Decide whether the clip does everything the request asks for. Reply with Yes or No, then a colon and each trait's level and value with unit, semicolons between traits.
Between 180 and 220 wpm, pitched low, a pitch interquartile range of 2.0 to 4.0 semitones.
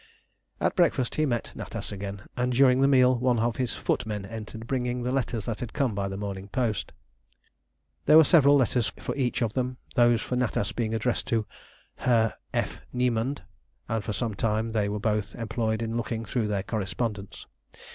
Yes: average, 185 wpm; low, 115 Hz; average, 2.9 semitones